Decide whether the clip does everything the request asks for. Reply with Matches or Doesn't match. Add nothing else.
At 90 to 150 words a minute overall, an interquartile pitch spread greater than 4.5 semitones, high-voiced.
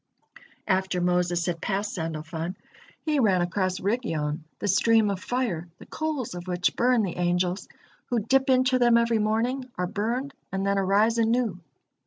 Doesn't match